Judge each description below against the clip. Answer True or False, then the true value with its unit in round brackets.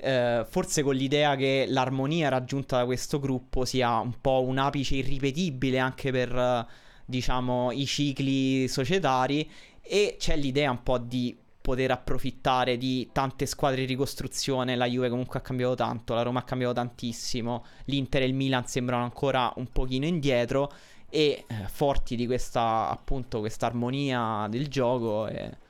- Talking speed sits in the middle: True (155 wpm)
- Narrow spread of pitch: True (1.9 semitones)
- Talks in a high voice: False (130 Hz)